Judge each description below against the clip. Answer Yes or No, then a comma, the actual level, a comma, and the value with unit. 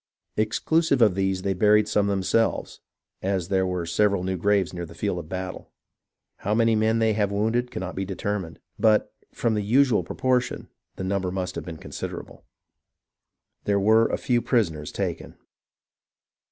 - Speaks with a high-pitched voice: No, low, 100 Hz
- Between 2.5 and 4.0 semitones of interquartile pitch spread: Yes, average, 3.0 semitones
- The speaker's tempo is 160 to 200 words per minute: Yes, average, 165 wpm